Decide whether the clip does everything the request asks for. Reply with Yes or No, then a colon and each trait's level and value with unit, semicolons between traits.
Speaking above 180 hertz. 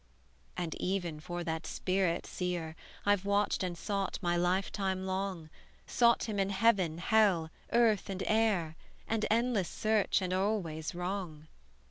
Yes: high, 190 Hz